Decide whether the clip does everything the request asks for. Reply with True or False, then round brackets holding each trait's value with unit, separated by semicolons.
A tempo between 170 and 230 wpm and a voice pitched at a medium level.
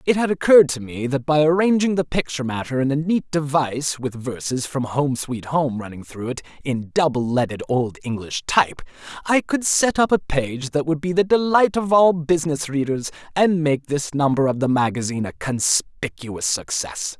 True (190 wpm; 145 Hz)